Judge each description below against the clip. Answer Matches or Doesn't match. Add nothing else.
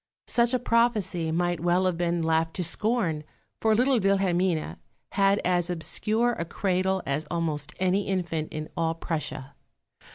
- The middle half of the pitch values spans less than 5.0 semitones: Matches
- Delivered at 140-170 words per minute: Matches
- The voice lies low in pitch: Doesn't match